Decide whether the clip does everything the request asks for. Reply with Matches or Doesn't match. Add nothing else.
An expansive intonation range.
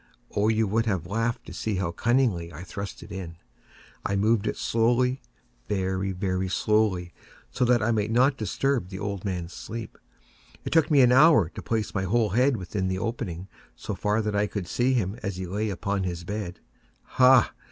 Doesn't match